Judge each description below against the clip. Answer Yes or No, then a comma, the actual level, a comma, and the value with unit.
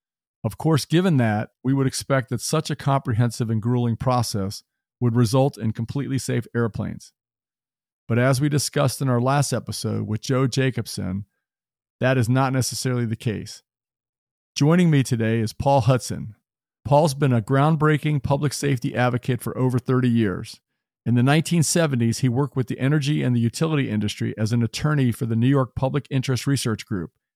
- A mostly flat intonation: No, average, 3.2 semitones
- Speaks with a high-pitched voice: No, low, 125 Hz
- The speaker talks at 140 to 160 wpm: No, average, 170 wpm